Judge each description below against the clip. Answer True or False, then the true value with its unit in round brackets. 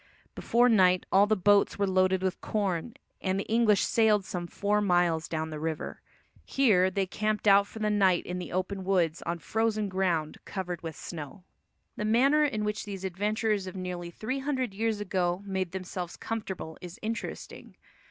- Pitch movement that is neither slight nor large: True (3.0 semitones)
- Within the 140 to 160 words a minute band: False (175 wpm)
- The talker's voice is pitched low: False (195 Hz)